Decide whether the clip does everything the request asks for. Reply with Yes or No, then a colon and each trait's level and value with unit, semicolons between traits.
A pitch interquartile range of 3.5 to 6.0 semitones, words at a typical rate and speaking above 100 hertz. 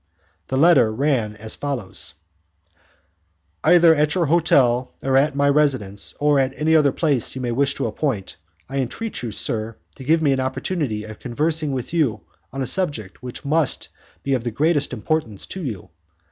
Yes: average, 4.3 semitones; average, 175 wpm; low, 135 Hz